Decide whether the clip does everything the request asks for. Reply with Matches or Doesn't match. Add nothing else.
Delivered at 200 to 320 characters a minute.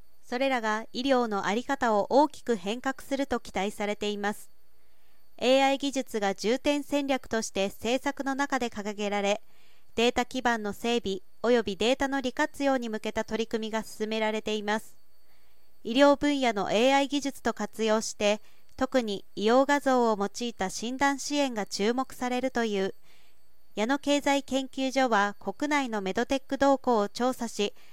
Matches